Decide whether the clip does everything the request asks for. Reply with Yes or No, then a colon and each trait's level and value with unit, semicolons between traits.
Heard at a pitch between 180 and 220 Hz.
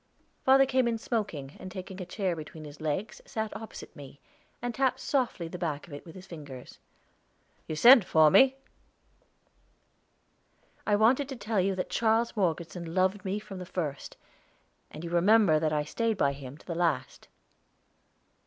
Yes: medium, 185 Hz